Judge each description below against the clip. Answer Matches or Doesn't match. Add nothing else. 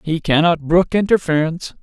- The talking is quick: Doesn't match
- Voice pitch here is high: Doesn't match